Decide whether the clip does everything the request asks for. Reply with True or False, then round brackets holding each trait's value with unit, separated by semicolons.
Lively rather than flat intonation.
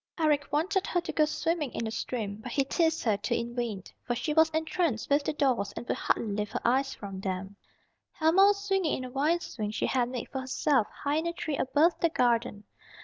True (5.7 semitones)